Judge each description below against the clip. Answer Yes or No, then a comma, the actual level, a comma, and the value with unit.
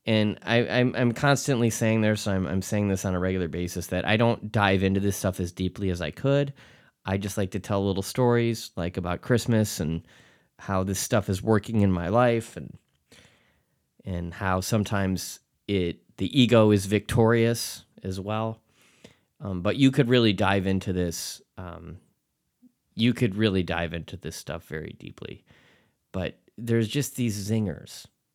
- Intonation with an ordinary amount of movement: Yes, average, 3.8 semitones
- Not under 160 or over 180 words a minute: Yes, average, 170 wpm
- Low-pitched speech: Yes, low, 100 Hz